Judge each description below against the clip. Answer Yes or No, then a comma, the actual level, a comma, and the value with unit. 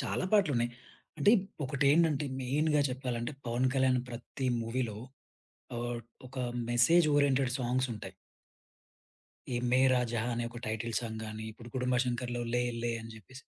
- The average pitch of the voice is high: No, low, 125 Hz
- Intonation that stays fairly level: Yes, narrow, 2.1 semitones